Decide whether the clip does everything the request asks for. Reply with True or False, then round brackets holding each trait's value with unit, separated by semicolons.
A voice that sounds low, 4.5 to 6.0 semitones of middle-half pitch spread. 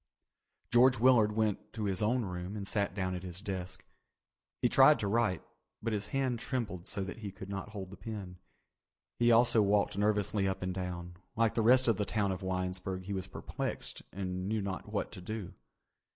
False (100 Hz; 3.1 semitones)